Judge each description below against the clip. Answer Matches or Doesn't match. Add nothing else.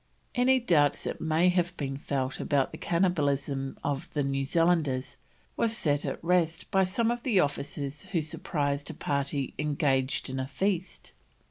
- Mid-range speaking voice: Matches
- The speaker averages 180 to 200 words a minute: Doesn't match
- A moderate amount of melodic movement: Matches